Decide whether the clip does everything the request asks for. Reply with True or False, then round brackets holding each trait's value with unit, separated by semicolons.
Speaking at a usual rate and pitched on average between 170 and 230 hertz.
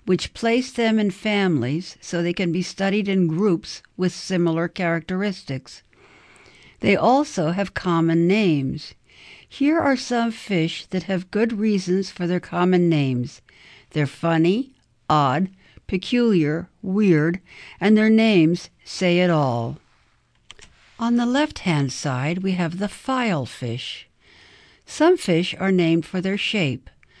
False (130 wpm; 185 Hz)